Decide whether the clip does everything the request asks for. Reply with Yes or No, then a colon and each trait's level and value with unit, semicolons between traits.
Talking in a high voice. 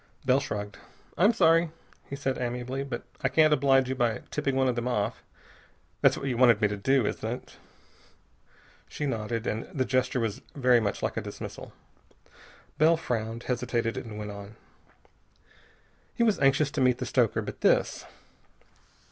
No: low, 125 Hz